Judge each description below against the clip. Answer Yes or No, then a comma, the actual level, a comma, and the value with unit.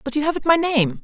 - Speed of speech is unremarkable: No, fast, 290 wpm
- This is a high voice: Yes, very high, 285 Hz